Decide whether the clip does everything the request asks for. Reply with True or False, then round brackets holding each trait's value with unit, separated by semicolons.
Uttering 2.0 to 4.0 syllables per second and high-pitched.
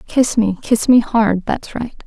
True (3.7 syllables/s; 220 Hz)